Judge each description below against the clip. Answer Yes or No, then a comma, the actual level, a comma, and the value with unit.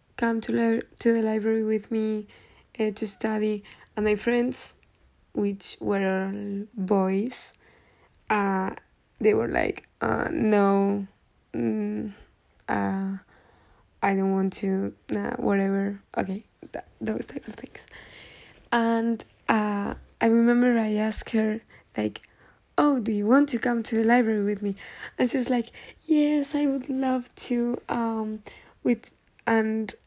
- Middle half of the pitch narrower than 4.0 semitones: Yes, average, 2.9 semitones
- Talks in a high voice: Yes, high, 220 Hz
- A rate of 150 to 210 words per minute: No, average, 135 wpm